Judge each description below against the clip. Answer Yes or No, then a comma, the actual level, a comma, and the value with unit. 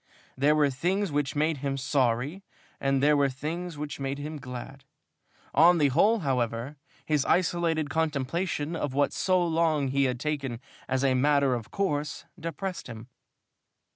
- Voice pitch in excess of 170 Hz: No, medium, 145 Hz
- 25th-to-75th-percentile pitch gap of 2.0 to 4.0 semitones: Yes, average, 3.3 semitones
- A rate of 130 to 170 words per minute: Yes, average, 160 wpm